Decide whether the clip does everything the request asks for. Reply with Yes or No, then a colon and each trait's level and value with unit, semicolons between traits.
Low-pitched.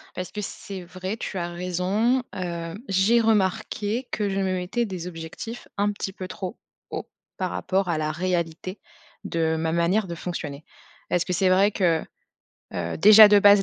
No: medium, 185 Hz